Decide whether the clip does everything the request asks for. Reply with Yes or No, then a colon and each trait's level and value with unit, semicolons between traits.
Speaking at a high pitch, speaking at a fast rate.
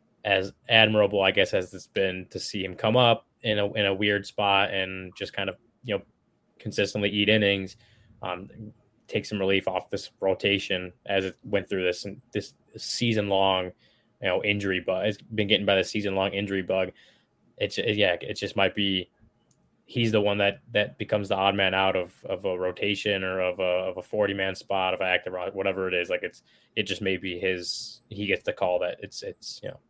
No: low, 100 Hz; fast, 215 wpm